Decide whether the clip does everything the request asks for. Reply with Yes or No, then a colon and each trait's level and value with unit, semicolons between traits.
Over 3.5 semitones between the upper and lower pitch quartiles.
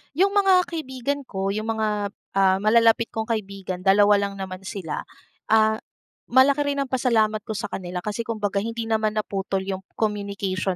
No: average, 2.8 semitones